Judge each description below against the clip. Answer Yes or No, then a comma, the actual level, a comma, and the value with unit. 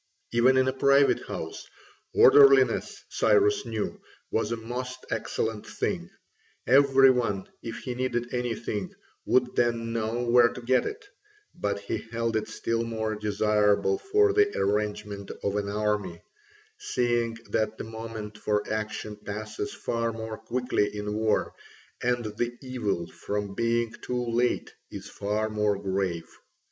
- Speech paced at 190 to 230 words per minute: No, average, 140 wpm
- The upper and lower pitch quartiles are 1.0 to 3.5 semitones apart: Yes, average, 2.9 semitones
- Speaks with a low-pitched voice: Yes, low, 115 Hz